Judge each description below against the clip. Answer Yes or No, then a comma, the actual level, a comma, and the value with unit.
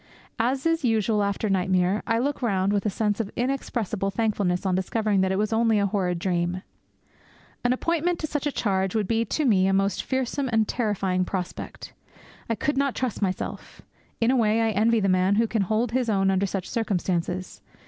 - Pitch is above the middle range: Yes, high, 210 Hz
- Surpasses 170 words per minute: Yes, average, 200 wpm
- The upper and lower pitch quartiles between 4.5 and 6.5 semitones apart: No, average, 3.5 semitones